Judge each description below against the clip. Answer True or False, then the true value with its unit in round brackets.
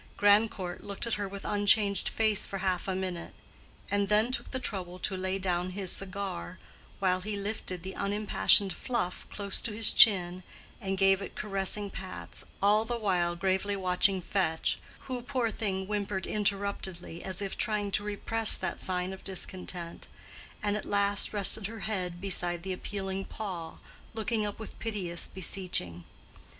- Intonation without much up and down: True (2.1 semitones)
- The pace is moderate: True (160 wpm)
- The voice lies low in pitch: False (195 Hz)